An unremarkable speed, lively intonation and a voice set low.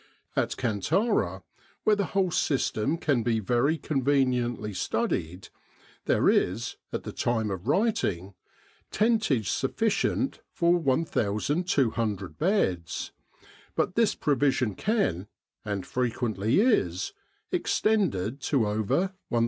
No: slow, 105 wpm; wide, 8.7 semitones; low, 125 Hz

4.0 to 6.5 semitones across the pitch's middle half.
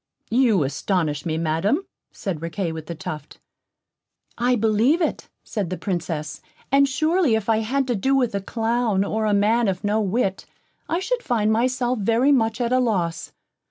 Yes: average, 5.1 semitones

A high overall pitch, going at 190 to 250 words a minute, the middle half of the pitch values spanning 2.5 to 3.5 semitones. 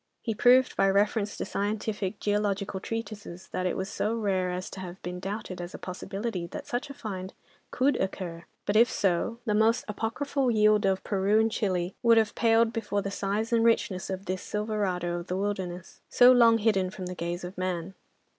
Yes: high, 200 Hz; average, 195 wpm; average, 3.2 semitones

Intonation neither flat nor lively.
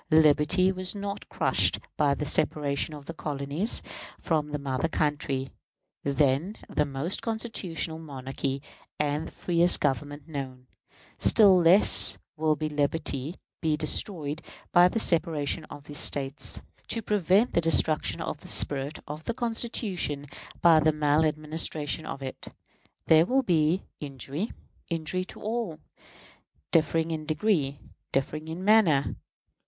Yes: average, 3.5 semitones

